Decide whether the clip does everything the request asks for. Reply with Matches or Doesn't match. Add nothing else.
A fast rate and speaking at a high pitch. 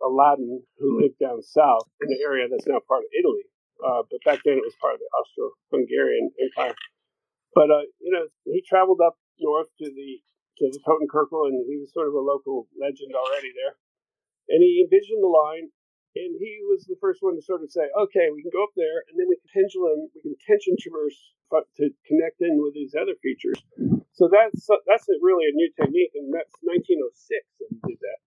Matches